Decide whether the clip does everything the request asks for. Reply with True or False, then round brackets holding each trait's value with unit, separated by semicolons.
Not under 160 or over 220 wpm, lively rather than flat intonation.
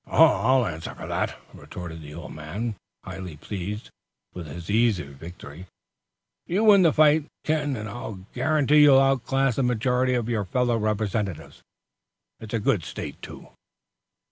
False (145 wpm; 6.8 semitones)